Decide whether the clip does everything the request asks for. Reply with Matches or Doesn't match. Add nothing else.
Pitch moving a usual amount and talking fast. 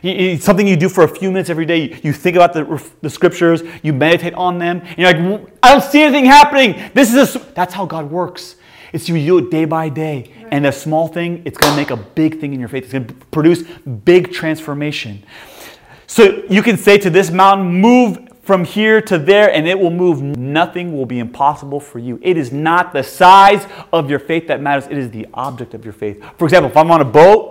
Matches